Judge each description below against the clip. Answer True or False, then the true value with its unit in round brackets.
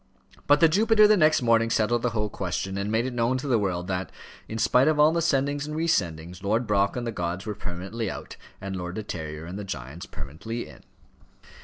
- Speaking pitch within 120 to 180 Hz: False (110 Hz)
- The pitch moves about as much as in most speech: False (6.1 semitones)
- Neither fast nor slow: False (225 wpm)